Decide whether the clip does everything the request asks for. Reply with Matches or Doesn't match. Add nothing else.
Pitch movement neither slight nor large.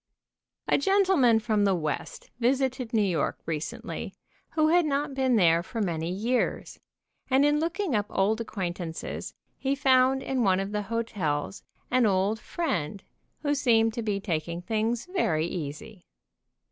Doesn't match